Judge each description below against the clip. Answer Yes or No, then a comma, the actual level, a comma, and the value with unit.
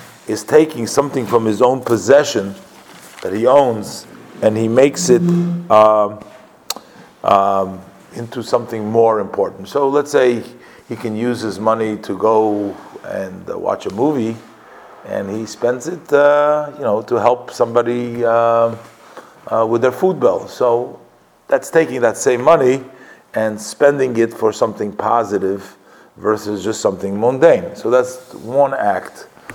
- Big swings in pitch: No, average, 3.7 semitones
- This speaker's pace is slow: No, average, 145 wpm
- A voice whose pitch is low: Yes, low, 120 Hz